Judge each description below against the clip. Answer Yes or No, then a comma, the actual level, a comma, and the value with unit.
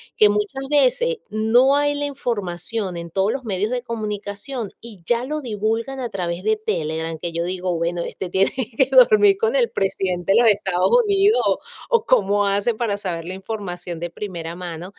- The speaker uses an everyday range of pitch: No, wide, 5.8 semitones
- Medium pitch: No, high, 210 Hz